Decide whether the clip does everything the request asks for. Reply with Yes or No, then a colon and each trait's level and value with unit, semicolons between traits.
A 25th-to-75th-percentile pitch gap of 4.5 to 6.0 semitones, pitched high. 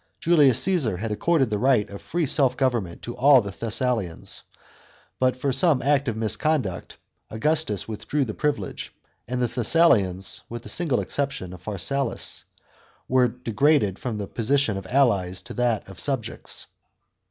No: average, 5.1 semitones; low, 125 Hz